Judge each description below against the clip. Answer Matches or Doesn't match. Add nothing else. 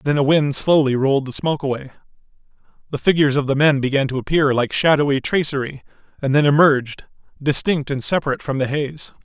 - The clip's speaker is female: Doesn't match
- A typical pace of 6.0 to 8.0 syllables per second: Matches